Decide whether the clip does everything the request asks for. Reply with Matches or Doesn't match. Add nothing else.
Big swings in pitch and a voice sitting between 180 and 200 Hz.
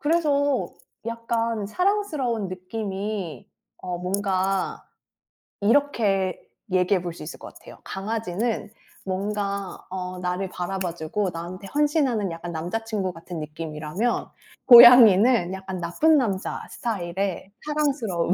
Doesn't match